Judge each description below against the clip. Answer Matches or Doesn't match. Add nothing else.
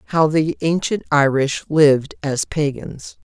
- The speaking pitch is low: Doesn't match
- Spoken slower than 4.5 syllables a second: Matches